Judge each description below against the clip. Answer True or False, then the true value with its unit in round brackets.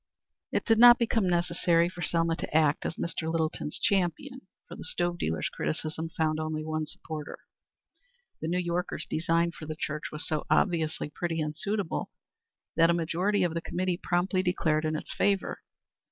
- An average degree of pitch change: False (2.3 semitones)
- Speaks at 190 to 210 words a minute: False (170 wpm)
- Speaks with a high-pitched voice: False (165 Hz)